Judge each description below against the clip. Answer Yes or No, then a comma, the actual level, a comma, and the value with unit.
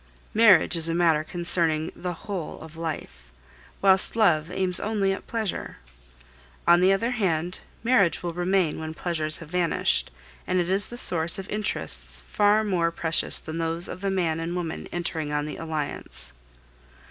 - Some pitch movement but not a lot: Yes, average, 3.2 semitones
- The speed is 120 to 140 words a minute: No, average, 165 wpm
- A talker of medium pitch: Yes, medium, 175 Hz